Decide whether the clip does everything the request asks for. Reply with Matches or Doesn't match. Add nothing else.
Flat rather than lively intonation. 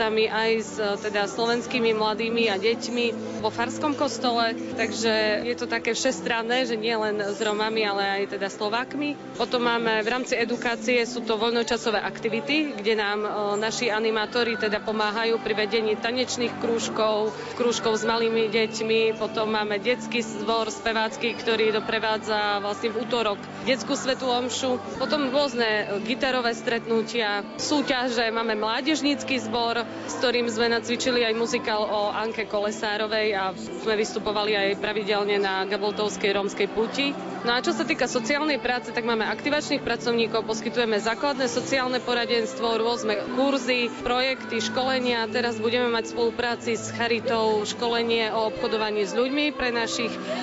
Matches